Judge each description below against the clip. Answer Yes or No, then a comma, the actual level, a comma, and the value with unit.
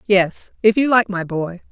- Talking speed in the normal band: No, fast, 210 wpm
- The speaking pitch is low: No, high, 200 Hz